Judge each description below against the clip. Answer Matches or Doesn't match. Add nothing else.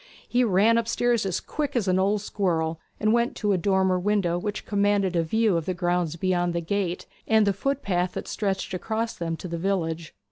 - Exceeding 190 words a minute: Matches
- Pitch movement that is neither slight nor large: Matches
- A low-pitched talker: Doesn't match